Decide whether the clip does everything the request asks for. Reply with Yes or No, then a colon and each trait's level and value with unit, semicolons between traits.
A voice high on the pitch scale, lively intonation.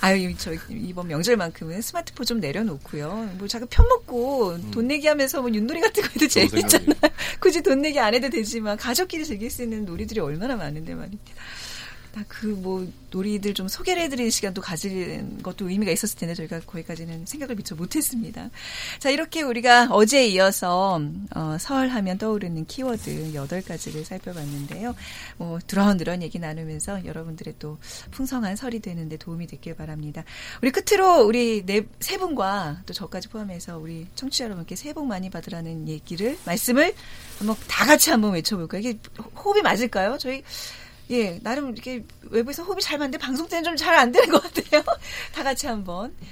Yes: high, 215 Hz; wide, 7.2 semitones